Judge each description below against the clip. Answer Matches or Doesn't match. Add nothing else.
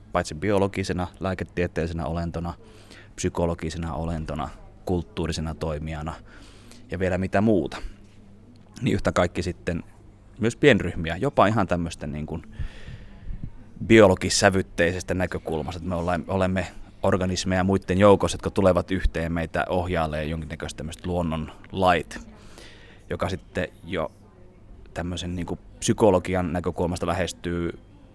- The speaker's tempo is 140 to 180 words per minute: Doesn't match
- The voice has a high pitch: Doesn't match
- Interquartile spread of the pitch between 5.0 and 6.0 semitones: Doesn't match